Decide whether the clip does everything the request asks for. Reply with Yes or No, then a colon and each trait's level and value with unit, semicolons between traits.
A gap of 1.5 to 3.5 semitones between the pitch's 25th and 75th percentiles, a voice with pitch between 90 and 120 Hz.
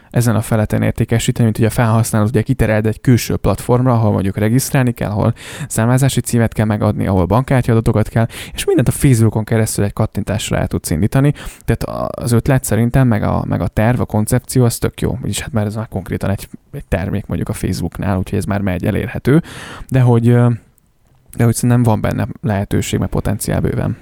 Yes: average, 2.8 semitones; low, 110 Hz